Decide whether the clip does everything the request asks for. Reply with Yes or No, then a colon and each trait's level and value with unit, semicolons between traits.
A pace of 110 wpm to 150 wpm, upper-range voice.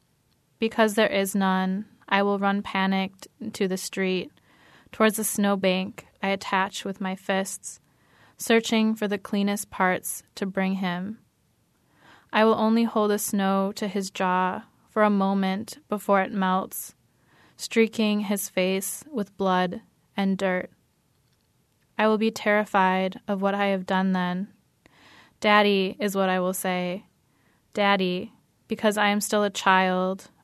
Yes: average, 145 wpm; high, 195 Hz